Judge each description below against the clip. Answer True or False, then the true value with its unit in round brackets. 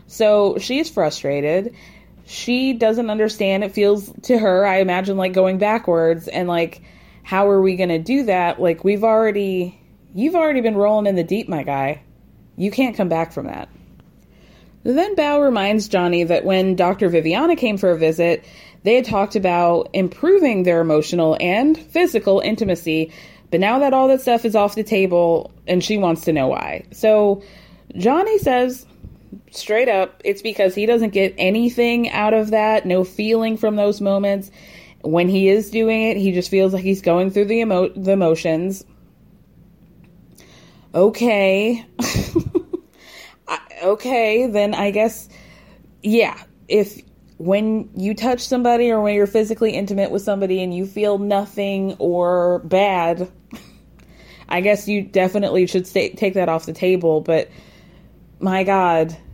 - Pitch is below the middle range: False (200 Hz)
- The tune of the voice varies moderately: True (3.4 semitones)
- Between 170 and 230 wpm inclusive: False (155 wpm)